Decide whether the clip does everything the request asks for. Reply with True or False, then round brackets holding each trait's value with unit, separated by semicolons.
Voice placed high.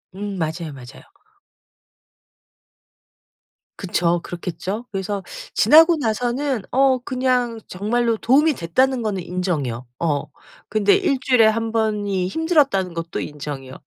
True (210 Hz)